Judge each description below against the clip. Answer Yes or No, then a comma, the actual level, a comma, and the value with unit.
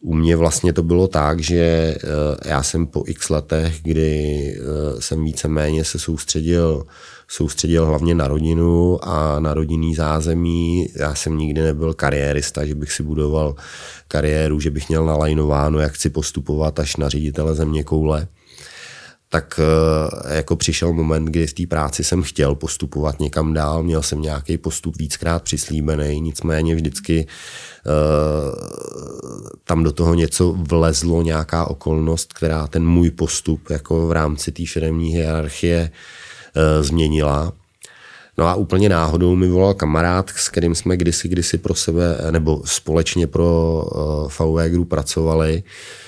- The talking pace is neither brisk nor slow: Yes, average, 140 wpm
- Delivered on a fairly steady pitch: Yes, narrow, 1.6 semitones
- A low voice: Yes, very low, 80 Hz